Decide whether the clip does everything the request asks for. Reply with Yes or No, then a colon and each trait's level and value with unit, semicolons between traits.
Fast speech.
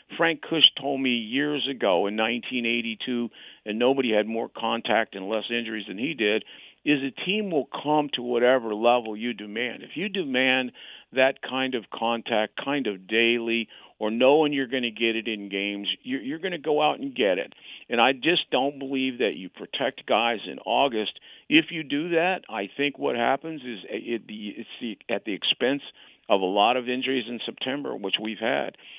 No: average, 185 wpm